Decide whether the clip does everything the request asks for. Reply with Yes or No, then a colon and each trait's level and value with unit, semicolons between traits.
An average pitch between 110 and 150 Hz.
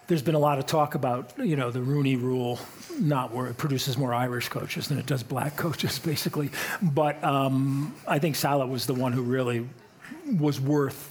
Yes: medium, 140 Hz